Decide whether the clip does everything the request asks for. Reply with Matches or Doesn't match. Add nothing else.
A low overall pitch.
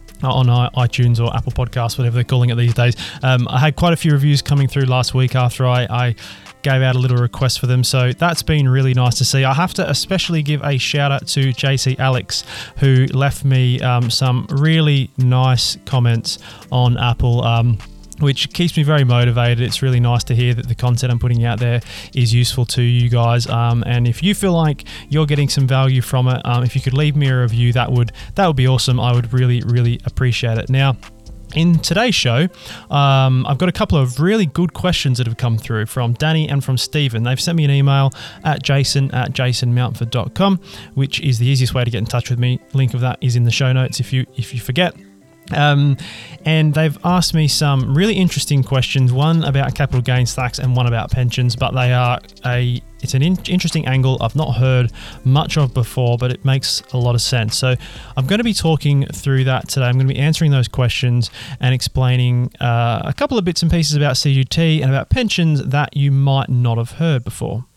Matches